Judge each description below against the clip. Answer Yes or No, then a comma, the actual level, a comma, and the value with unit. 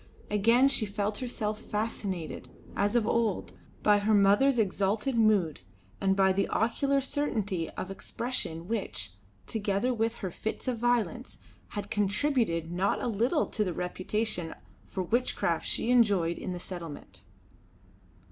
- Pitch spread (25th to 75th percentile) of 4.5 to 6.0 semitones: No, average, 3.5 semitones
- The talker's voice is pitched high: Yes, high, 210 Hz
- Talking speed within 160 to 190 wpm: No, average, 140 wpm